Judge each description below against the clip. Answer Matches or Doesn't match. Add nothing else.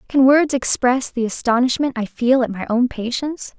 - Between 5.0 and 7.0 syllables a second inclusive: Matches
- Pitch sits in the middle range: Doesn't match